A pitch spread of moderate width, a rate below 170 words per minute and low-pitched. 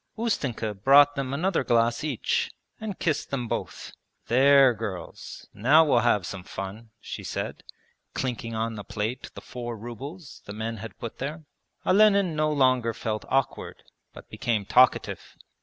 Yes: average, 4.4 semitones; average, 150 wpm; low, 125 Hz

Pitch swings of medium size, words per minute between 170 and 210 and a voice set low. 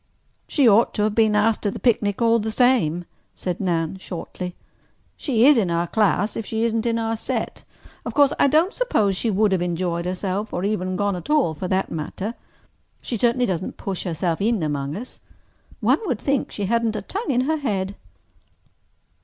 No: average, 4.2 semitones; average, 190 wpm; high, 210 Hz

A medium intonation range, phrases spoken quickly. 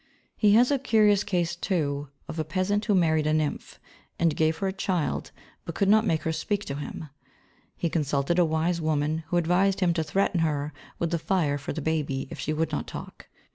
Yes: average, 3.6 semitones; fast, 215 wpm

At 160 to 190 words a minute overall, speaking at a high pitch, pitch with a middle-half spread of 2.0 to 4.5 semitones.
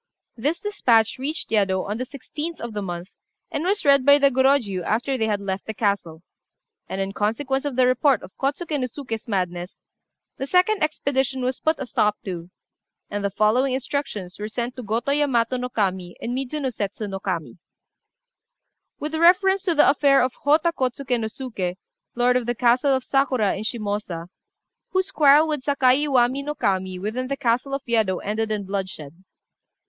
No: average, 180 wpm; high, 245 Hz; average, 5.3 semitones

